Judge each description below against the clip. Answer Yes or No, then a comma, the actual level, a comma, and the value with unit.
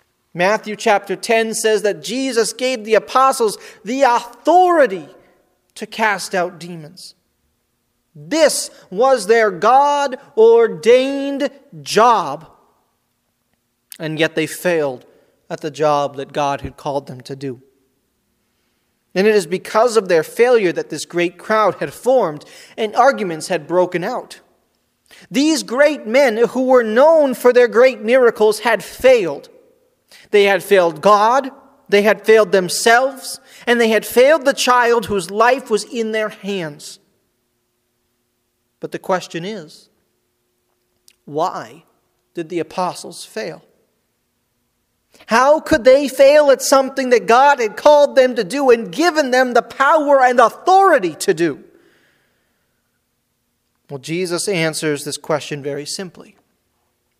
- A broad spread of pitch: Yes, wide, 7.5 semitones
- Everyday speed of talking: No, slow, 130 wpm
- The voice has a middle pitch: No, high, 220 Hz